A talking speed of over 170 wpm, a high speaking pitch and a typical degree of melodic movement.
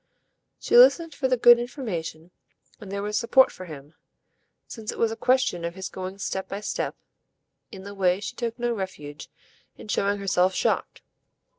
Yes: average, 180 wpm; high, 200 Hz; average, 4.4 semitones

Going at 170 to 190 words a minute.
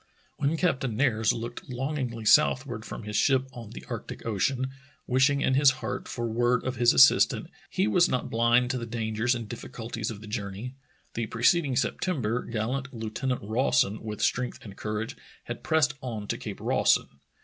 Yes: average, 180 wpm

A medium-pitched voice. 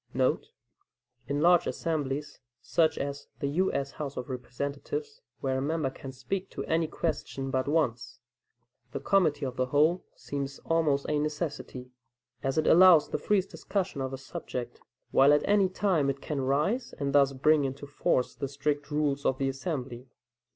Yes: medium, 145 Hz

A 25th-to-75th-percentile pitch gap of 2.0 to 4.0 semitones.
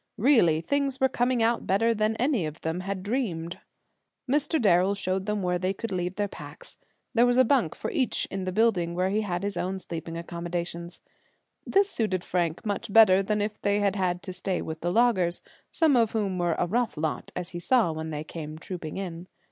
No: average, 4.6 semitones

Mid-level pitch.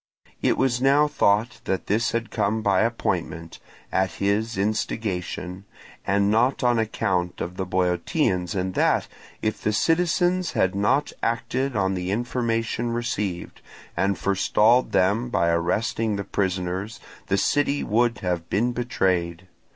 No: low, 105 Hz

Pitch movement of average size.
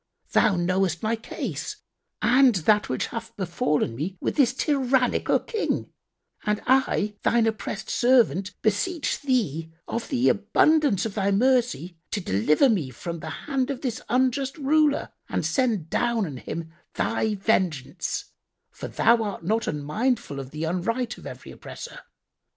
No: wide, 6.5 semitones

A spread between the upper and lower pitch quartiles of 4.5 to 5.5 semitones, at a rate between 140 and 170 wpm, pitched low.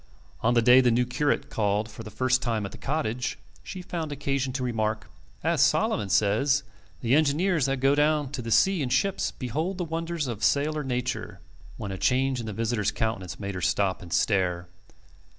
No: average, 5.1 semitones; average, 195 wpm; low, 125 Hz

